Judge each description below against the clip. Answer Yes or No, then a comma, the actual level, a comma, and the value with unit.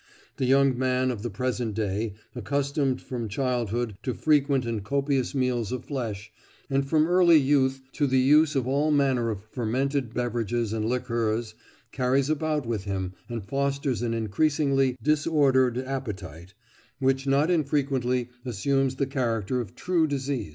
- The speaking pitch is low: Yes, low, 130 Hz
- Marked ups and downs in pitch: No, average, 3.2 semitones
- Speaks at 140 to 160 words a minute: Yes, average, 150 wpm